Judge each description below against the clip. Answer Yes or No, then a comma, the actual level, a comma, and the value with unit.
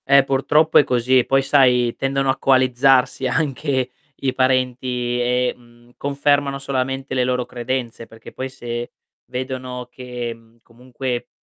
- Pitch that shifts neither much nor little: No, narrow, 1.7 semitones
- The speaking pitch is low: Yes, low, 130 Hz